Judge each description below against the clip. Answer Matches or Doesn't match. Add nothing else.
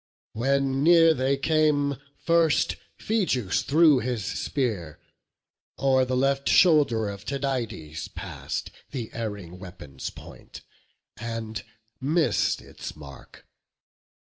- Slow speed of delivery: Matches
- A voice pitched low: Matches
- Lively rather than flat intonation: Doesn't match